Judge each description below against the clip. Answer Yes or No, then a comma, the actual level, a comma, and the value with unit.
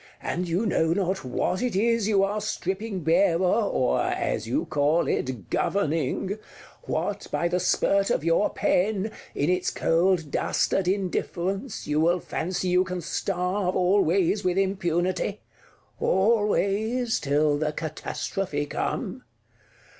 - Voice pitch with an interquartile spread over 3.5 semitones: No, average, 3.1 semitones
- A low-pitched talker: No, medium, 185 Hz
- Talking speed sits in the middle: No, slow, 130 wpm